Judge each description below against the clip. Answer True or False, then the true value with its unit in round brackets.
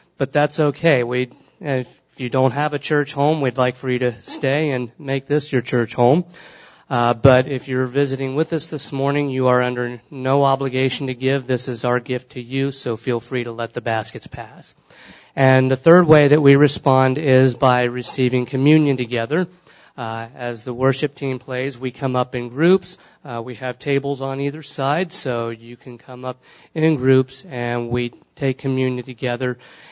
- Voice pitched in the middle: False (130 Hz)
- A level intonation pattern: True (2.2 semitones)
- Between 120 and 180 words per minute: False (190 wpm)